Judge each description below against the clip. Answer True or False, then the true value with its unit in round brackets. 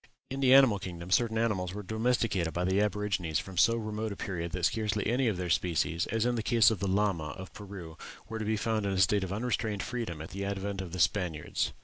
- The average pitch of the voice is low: True (100 Hz)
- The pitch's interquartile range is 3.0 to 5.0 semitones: True (3.4 semitones)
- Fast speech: True (240 wpm)